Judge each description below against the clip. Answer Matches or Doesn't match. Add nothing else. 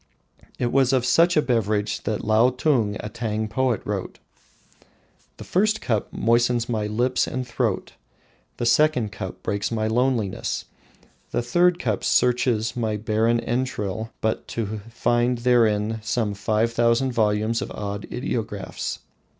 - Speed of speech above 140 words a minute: Doesn't match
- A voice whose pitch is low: Matches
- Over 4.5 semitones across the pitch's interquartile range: Doesn't match